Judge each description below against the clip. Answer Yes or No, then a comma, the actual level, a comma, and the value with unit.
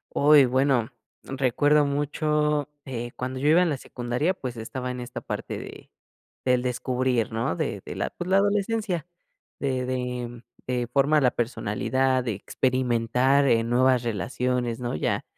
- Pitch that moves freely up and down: No, average, 2.8 semitones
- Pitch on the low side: Yes, low, 130 Hz